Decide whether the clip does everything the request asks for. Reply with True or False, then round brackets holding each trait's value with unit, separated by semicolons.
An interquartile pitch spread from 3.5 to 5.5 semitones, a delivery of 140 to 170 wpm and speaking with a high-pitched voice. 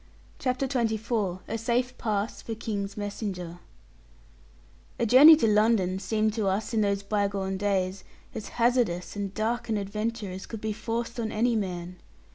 False (2.7 semitones; 155 wpm; 215 Hz)